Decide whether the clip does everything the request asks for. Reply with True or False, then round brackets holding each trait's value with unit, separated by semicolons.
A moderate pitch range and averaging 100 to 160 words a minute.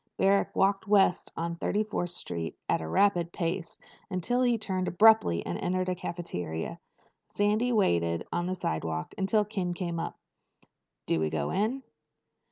True (3.7 semitones; 155 wpm)